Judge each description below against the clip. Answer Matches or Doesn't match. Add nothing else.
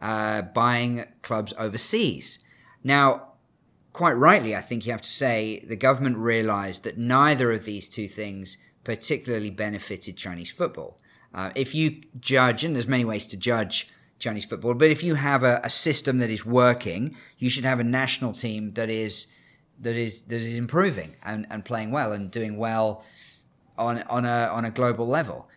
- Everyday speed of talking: Matches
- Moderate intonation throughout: Matches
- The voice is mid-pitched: Doesn't match